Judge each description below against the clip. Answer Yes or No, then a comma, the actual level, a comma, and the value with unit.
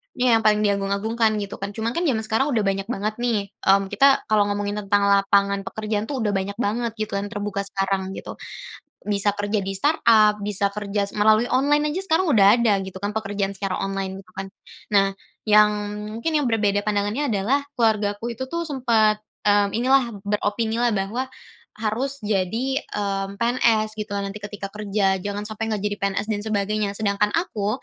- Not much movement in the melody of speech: Yes, narrow, 2.2 semitones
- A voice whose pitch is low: No, high, 210 Hz